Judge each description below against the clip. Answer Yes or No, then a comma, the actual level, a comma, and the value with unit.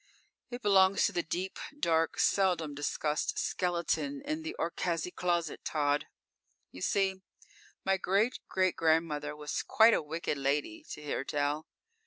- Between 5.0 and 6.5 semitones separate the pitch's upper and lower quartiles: No, average, 4.4 semitones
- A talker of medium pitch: Yes, medium, 170 Hz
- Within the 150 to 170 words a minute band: No, average, 140 wpm